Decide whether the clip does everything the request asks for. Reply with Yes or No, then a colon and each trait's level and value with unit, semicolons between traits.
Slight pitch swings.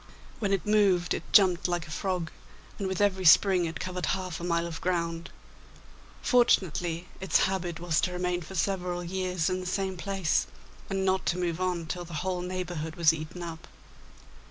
Yes: narrow, 1.9 semitones